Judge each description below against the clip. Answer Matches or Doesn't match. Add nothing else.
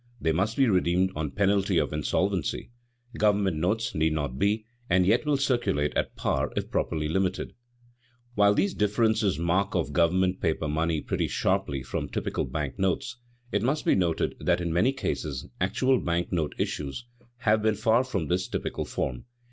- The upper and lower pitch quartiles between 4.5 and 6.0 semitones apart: Matches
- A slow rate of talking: Doesn't match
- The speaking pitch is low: Matches